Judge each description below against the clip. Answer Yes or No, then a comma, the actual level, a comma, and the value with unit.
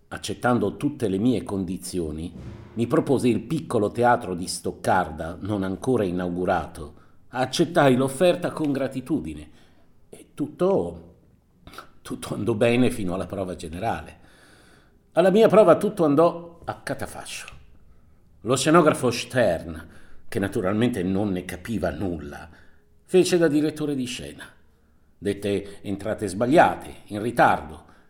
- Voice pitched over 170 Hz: No, low, 100 Hz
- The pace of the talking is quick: No, slow, 115 wpm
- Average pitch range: No, wide, 6.4 semitones